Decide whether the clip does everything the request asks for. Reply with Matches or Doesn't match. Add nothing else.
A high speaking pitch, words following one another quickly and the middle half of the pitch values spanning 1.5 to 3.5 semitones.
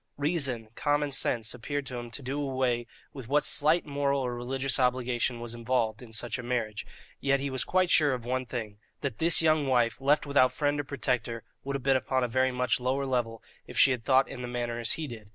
Doesn't match